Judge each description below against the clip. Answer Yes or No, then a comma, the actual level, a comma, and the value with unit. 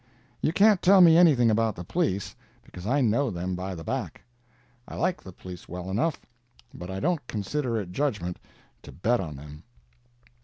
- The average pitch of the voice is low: Yes, low, 110 Hz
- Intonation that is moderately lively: No, wide, 8.6 semitones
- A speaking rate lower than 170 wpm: No, average, 180 wpm